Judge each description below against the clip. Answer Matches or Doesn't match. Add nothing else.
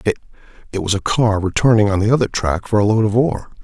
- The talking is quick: Matches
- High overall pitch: Doesn't match